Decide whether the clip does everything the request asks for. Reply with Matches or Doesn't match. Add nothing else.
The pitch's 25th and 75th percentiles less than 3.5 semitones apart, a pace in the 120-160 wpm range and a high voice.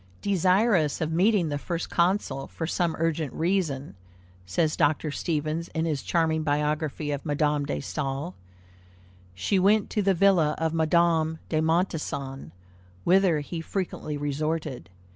Doesn't match